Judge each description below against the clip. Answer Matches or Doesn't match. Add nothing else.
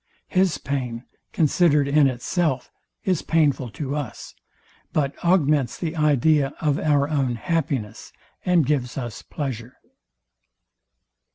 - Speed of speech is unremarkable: Doesn't match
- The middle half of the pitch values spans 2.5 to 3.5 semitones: Matches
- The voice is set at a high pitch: Doesn't match